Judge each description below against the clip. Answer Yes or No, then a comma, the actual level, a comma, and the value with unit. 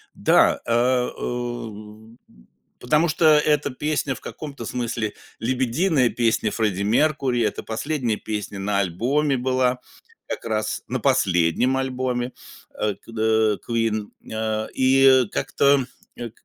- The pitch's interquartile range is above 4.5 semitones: No, average, 3.3 semitones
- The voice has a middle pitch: No, low, 120 Hz